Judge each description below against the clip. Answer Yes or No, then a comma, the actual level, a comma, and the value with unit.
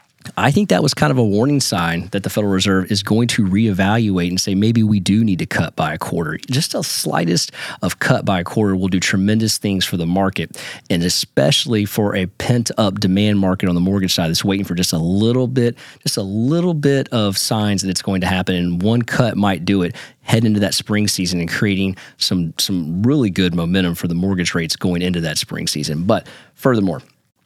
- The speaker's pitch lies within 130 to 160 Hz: No, low, 100 Hz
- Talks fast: Yes, fast, 220 wpm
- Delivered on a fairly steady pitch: No, average, 3.3 semitones